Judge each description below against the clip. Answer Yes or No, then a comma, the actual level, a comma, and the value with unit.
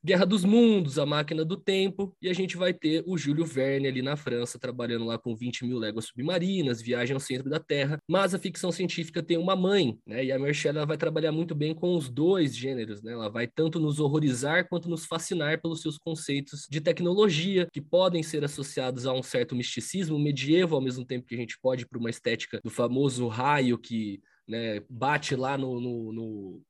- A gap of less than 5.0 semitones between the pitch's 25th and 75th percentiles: No, wide, 5.4 semitones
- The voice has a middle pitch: Yes, medium, 145 Hz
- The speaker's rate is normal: No, fast, 210 wpm